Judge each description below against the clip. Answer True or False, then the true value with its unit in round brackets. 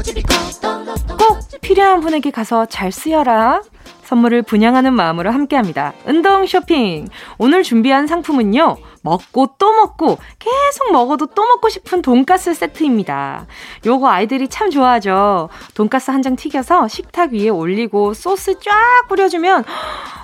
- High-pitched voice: True (270 Hz)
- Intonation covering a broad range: True (8.4 semitones)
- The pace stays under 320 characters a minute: True (290 characters per minute)